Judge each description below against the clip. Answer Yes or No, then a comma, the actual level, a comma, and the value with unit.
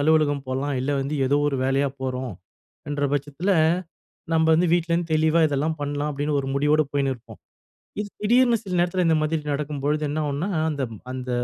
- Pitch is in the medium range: Yes, medium, 145 Hz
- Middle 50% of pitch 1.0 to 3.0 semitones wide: Yes, narrow, 2.4 semitones